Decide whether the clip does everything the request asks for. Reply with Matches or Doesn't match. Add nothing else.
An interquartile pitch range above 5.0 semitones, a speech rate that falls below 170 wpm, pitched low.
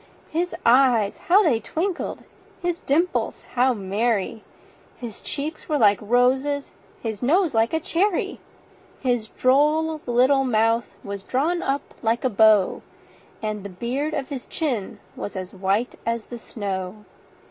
Doesn't match